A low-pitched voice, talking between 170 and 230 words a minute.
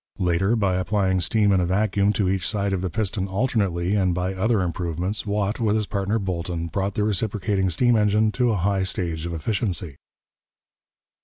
Yes: very low, 95 Hz; average, 180 wpm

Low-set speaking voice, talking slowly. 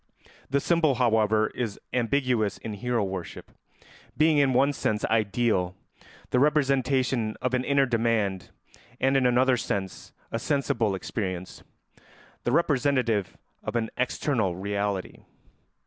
Yes: low, 120 Hz; slow, 120 wpm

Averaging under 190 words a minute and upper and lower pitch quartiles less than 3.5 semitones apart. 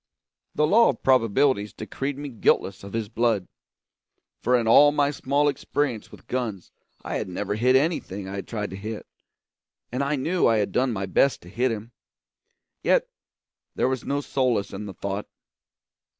No: average, 175 wpm; average, 5.2 semitones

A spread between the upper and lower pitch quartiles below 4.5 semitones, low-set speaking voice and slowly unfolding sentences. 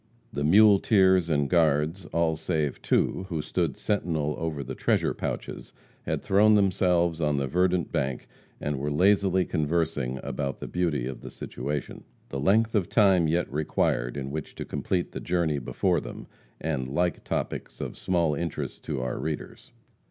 No: average, 4.0 semitones; very low, 80 Hz; average, 160 wpm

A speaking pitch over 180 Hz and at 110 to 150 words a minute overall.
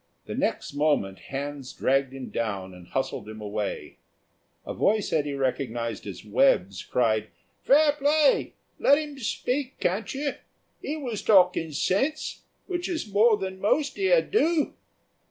Yes: high, 190 Hz; average, 140 wpm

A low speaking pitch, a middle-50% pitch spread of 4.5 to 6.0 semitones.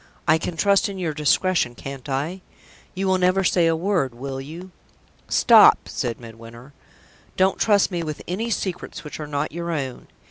No: medium, 165 Hz; average, 5.3 semitones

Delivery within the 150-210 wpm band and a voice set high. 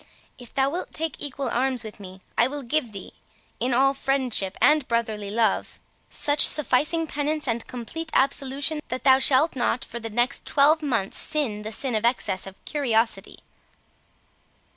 Yes: average, 165 wpm; very high, 260 Hz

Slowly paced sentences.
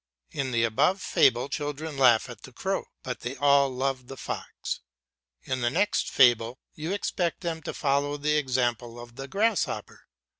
No: average, 165 wpm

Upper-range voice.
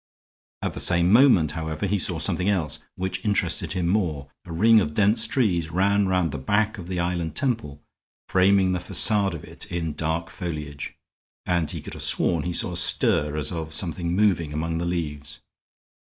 No: very low, 85 Hz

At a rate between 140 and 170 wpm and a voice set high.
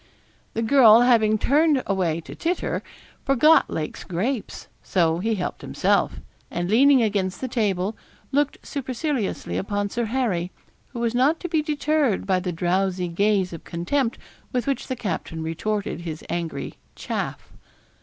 Yes: average, 145 wpm; high, 215 Hz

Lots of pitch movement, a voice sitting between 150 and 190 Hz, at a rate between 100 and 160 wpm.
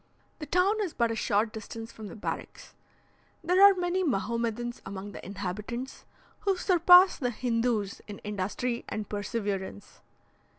No: wide, 8.2 semitones; high, 230 Hz; average, 140 wpm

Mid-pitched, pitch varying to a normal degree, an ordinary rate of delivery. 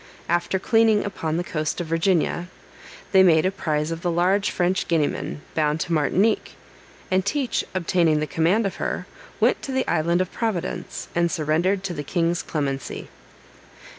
Yes: medium, 175 Hz; average, 3.1 semitones; average, 165 wpm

